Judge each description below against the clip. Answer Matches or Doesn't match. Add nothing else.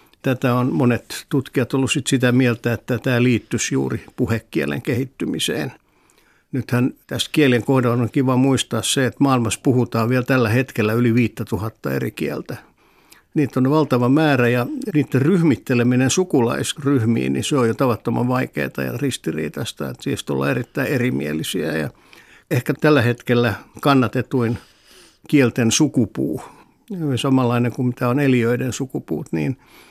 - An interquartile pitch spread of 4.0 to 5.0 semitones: Doesn't match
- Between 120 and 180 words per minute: Matches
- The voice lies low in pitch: Matches